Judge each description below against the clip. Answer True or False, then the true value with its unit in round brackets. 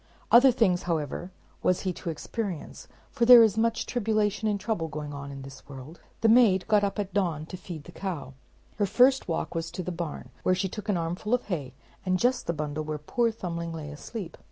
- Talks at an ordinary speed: False (225 wpm)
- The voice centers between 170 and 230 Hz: True (185 Hz)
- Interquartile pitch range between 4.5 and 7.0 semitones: True (5.2 semitones)